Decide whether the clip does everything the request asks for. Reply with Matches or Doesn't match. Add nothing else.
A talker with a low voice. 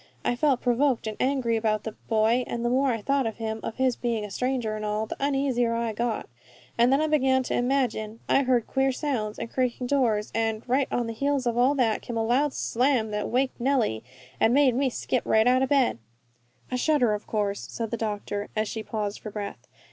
Doesn't match